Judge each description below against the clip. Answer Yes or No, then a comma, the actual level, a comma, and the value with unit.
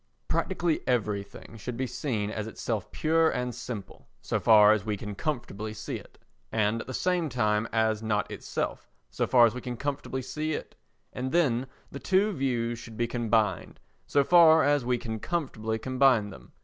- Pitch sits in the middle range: No, low, 120 Hz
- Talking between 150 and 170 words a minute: No, average, 180 wpm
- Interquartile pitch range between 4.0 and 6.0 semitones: Yes, average, 4.3 semitones